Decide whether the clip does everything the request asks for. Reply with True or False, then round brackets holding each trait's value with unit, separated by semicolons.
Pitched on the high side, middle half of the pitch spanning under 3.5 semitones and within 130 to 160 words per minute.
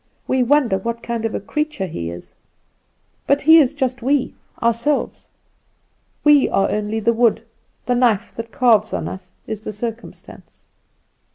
False (235 Hz; 3.8 semitones; 155 wpm)